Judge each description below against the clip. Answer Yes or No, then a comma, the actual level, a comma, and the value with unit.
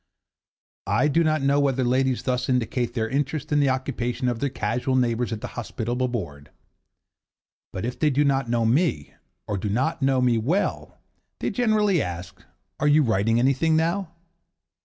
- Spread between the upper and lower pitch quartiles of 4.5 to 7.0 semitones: No, average, 3.9 semitones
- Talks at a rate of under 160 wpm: No, average, 170 wpm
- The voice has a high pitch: No, low, 130 Hz